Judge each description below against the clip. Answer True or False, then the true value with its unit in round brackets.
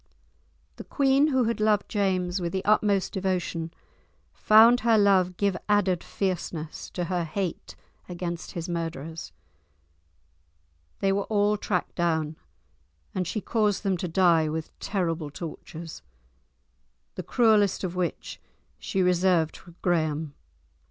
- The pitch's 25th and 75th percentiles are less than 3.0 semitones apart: False (3.4 semitones)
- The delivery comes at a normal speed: False (125 wpm)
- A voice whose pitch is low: False (185 Hz)